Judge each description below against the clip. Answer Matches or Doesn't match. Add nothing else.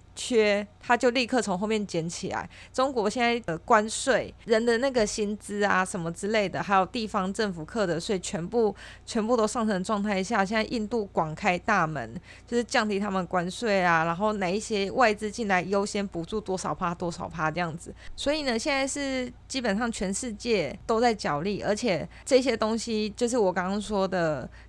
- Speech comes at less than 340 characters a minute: Matches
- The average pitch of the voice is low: Doesn't match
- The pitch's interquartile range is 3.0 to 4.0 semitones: Matches